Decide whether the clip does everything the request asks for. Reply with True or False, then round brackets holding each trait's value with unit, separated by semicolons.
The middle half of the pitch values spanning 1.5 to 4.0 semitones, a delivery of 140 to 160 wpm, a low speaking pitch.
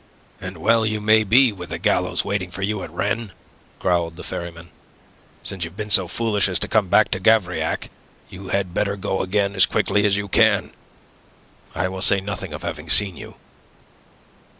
False (2.6 semitones; 185 wpm; 95 Hz)